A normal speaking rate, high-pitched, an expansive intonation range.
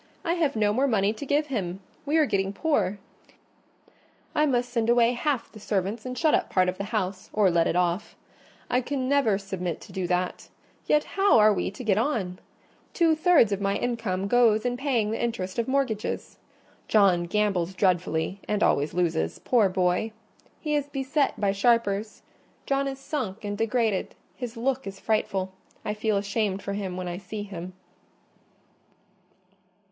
No: average, 165 wpm; high, 210 Hz; average, 4.7 semitones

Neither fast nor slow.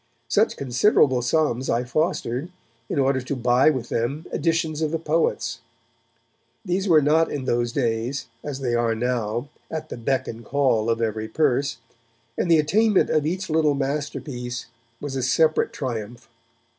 Yes: average, 155 wpm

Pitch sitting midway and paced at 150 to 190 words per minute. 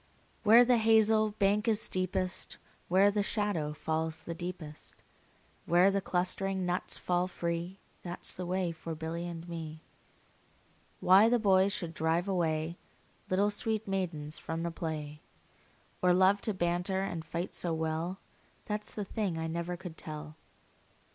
Yes: medium, 180 Hz; average, 155 wpm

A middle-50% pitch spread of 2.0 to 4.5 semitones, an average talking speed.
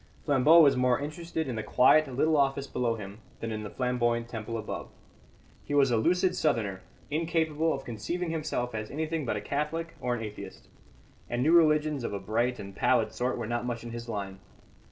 No: average, 5.0 semitones; average, 195 wpm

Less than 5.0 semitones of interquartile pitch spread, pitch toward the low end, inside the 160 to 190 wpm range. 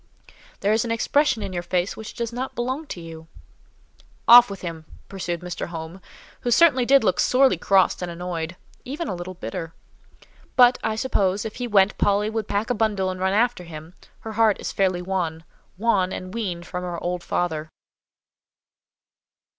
No: average, 4.5 semitones; high, 195 Hz; average, 170 wpm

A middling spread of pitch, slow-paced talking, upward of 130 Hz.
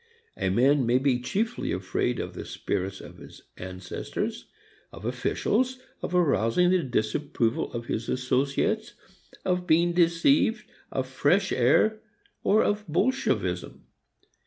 No: wide, 7.3 semitones; slow, 125 wpm; medium, 140 Hz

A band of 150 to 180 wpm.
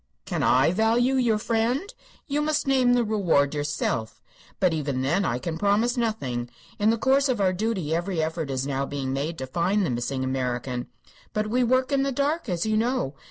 No: average, 200 wpm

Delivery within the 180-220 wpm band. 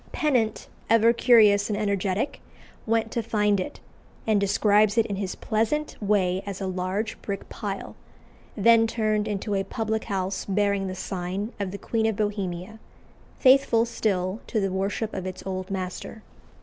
No: average, 160 wpm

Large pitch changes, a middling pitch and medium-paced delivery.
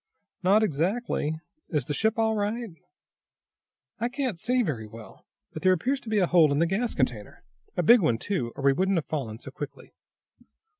Yes: wide, 7.2 semitones; medium, 180 Hz; average, 190 wpm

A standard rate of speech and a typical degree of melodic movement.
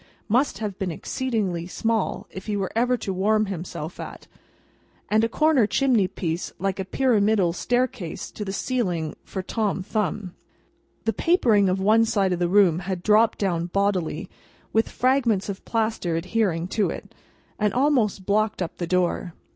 Yes: average, 165 wpm; average, 3.5 semitones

